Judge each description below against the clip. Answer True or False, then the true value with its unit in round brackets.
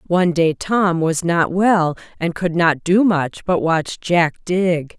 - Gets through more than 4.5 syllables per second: False (3.6 syllables/s)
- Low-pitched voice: False (170 Hz)